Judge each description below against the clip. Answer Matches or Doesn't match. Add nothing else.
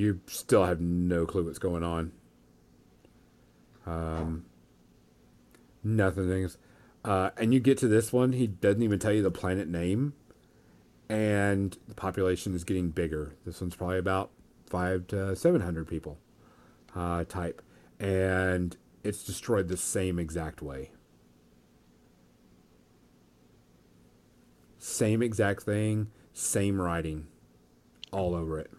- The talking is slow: Matches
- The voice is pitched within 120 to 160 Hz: Doesn't match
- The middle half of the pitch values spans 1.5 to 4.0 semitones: Doesn't match